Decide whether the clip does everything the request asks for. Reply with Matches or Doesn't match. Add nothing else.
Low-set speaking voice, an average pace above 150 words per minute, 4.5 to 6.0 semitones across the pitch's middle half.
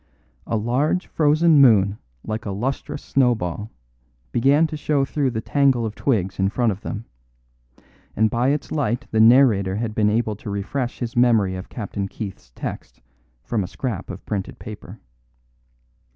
Matches